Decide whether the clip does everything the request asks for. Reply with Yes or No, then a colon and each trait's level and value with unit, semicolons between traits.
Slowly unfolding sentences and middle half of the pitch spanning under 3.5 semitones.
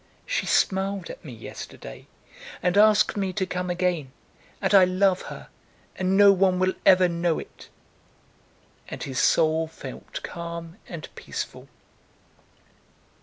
Yes: slow, 130 wpm; narrow, 2.4 semitones